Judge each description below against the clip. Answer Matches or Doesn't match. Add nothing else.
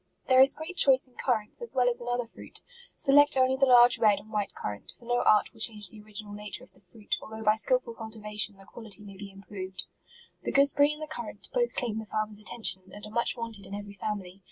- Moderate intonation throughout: Matches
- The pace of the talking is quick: Matches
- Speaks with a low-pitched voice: Doesn't match